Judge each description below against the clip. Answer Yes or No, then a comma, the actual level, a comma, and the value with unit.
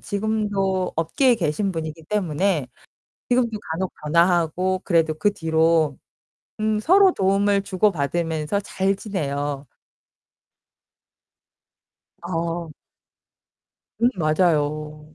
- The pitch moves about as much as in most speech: Yes, average, 4.3 semitones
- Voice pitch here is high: No, medium, 175 Hz